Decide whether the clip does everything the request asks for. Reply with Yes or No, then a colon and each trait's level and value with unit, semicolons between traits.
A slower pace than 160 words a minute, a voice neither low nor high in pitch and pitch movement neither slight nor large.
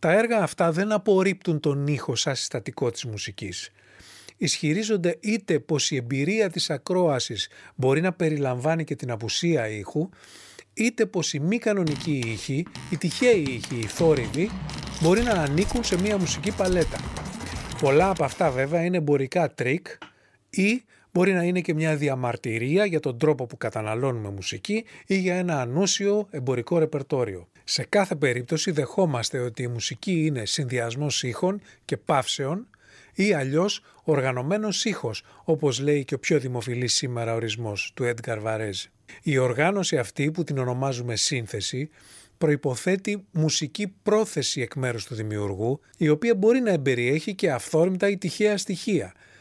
No: average, 150 wpm; medium, 155 Hz; wide, 6.7 semitones